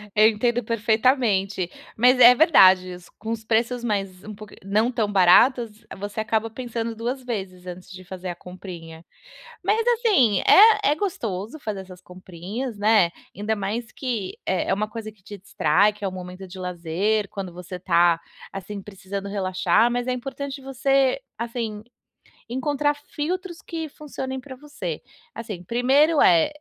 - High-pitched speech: Yes, high, 215 Hz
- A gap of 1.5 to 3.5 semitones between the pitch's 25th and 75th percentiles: No, average, 5.0 semitones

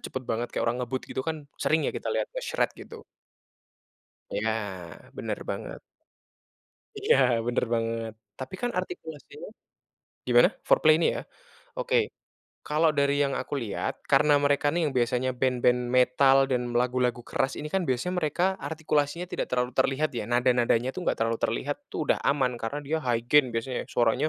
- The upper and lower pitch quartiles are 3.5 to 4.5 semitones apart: Yes, average, 3.8 semitones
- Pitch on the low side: Yes, low, 130 Hz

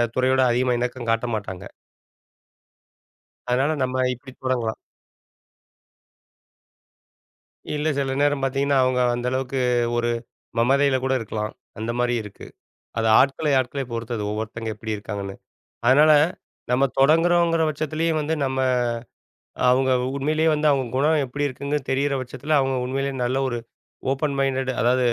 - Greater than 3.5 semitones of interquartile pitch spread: No, average, 2.7 semitones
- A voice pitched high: No, low, 130 Hz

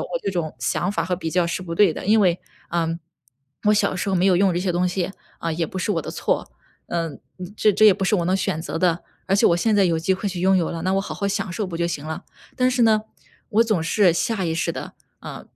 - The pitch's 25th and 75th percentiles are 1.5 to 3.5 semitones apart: Yes, average, 2.8 semitones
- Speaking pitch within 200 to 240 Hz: No, medium, 185 Hz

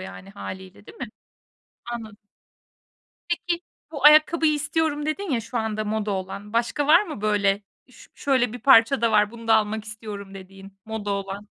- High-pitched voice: Yes, high, 220 Hz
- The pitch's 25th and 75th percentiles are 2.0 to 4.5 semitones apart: No, wide, 5.4 semitones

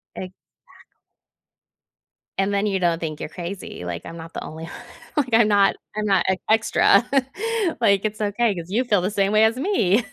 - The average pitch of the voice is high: Yes, high, 200 Hz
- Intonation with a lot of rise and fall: No, average, 3.5 semitones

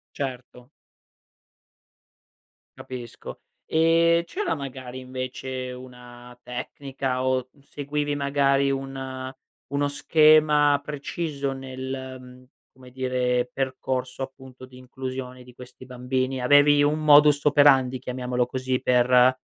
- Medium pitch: No, low, 130 Hz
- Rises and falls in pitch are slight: Yes, narrow, 1.9 semitones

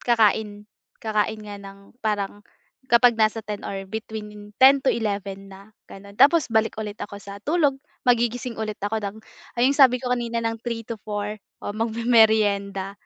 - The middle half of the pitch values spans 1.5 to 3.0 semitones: Yes, narrow, 2.4 semitones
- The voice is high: Yes, high, 220 Hz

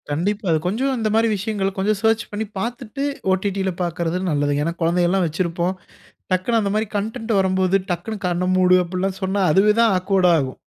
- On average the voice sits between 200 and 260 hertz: No, high, 190 Hz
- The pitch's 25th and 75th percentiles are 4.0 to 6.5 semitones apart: No, average, 3.3 semitones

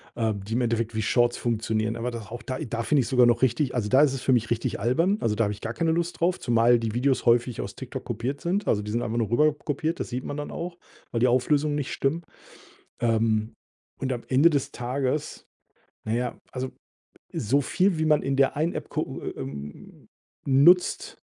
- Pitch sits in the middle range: No, low, 125 Hz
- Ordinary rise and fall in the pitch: Yes, average, 4.0 semitones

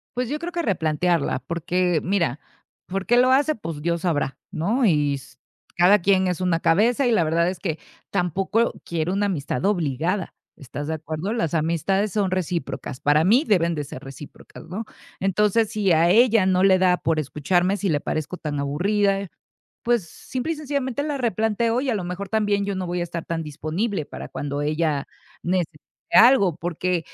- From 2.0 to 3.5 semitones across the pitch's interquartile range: No, average, 4.7 semitones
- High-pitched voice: No, medium, 180 Hz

